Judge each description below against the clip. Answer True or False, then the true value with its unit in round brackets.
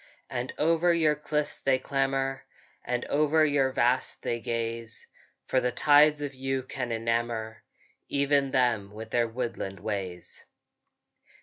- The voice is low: True (130 Hz)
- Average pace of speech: False (130 wpm)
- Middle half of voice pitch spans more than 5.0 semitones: False (3.6 semitones)